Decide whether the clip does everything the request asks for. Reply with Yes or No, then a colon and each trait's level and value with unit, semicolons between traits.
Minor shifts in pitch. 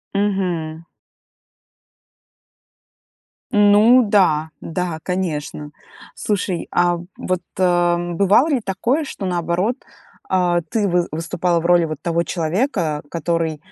No: average, 3.1 semitones